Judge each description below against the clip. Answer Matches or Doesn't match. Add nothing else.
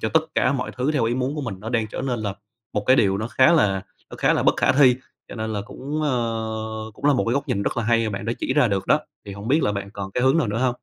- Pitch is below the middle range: Matches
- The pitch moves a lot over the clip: Doesn't match